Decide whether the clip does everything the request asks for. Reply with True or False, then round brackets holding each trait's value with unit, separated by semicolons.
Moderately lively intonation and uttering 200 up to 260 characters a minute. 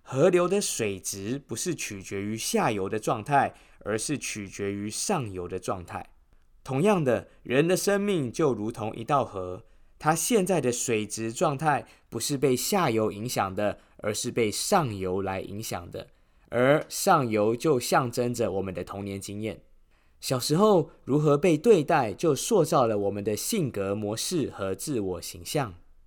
False (6.8 semitones; 235 characters per minute)